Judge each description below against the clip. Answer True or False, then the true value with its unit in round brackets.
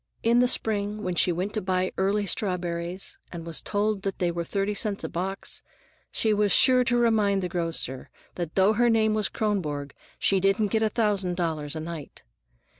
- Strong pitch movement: False (3.5 semitones)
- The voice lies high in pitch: True (195 Hz)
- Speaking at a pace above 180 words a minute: True (190 wpm)